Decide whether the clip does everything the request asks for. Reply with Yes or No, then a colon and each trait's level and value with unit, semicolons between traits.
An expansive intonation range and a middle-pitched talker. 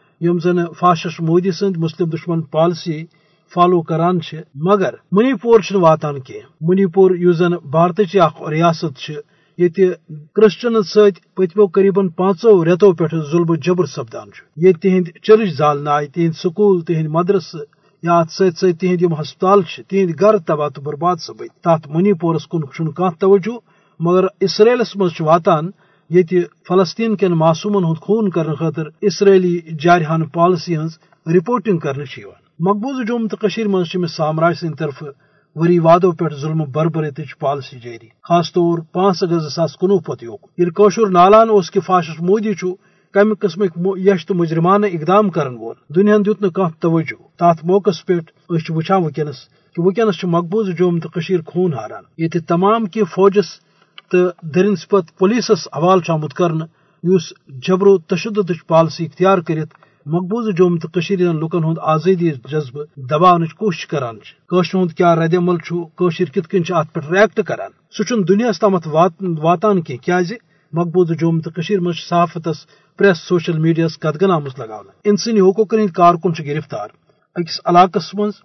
No: average, 3.2 semitones; medium, 175 Hz